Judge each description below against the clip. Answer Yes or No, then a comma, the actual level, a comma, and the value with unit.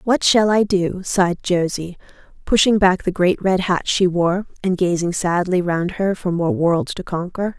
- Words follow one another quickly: No, average, 190 wpm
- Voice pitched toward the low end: No, medium, 180 Hz